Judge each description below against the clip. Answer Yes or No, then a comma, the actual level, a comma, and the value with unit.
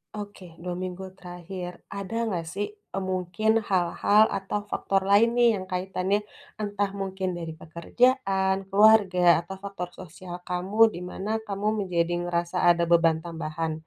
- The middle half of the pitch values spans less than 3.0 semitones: Yes, narrow, 2.5 semitones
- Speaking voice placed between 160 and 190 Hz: Yes, medium, 185 Hz